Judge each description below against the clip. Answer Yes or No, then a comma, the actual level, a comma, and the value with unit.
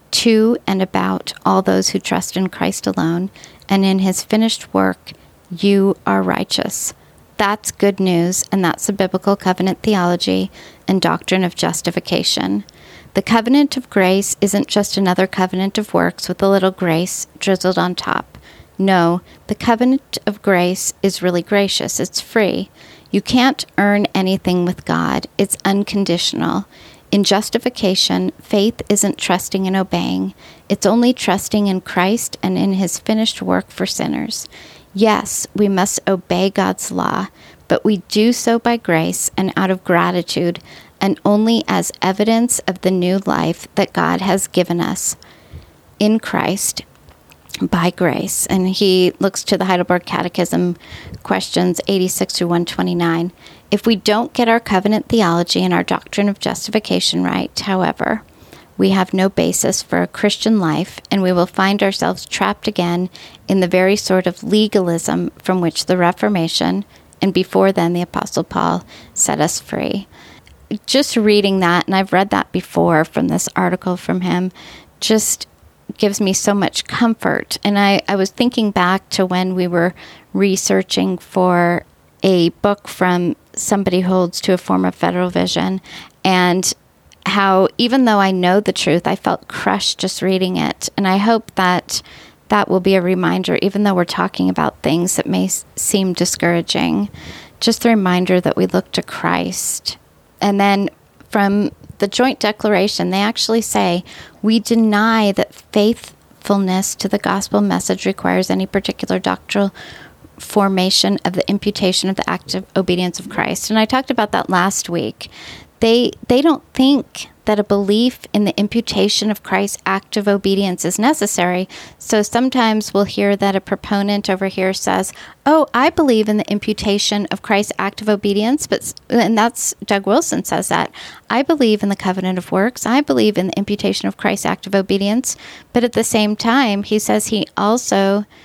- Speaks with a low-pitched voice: No, high, 195 Hz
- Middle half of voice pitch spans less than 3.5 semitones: Yes, average, 2.8 semitones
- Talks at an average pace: Yes, average, 160 wpm